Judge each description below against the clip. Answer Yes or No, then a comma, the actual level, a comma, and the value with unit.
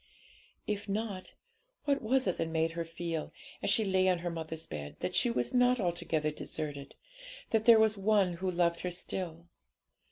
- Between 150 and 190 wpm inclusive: Yes, average, 180 wpm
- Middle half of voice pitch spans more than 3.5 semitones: Yes, average, 4.3 semitones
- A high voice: No, medium, 175 Hz